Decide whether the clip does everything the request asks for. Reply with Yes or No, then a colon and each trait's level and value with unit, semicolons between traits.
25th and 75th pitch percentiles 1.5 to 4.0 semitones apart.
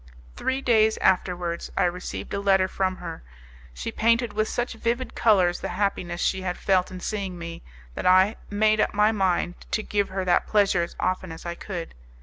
Yes: average, 3.2 semitones